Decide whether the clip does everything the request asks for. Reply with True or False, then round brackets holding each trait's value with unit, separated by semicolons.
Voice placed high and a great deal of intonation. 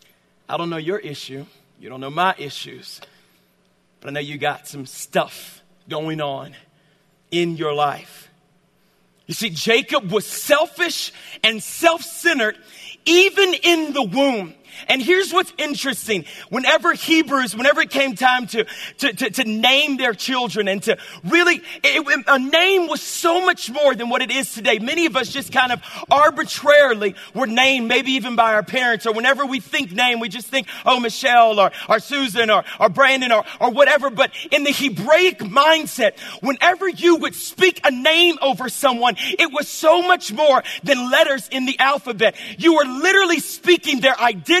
True (265 Hz; 6.5 semitones)